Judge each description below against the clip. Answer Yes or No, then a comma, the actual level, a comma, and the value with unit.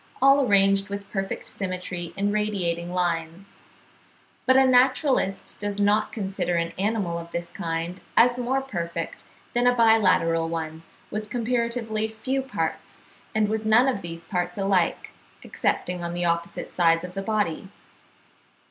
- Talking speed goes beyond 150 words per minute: No, average, 145 wpm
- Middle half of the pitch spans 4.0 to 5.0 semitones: Yes, average, 4.4 semitones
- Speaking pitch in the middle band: No, high, 195 Hz